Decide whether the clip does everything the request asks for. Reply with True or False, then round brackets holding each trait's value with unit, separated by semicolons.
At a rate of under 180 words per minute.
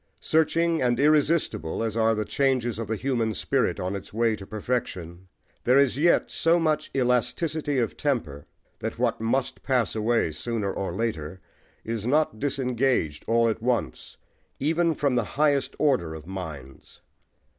True (155 wpm)